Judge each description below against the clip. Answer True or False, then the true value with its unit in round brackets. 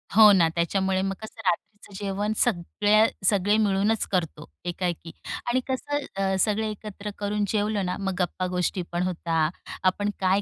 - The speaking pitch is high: True (195 Hz)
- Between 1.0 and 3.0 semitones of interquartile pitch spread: True (2.6 semitones)